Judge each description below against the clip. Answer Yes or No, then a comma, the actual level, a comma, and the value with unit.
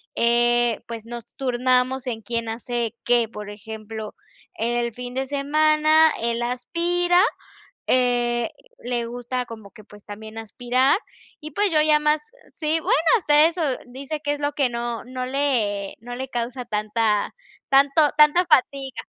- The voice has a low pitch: No, high, 245 Hz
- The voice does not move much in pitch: No, average, 3.8 semitones